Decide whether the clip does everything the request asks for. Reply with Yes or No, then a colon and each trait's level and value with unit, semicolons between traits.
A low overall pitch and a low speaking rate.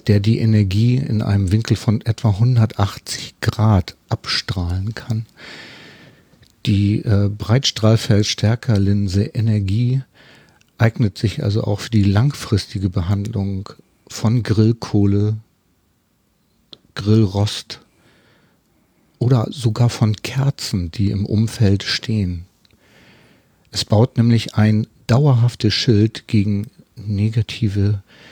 Yes: low, 110 Hz; slow, 90 wpm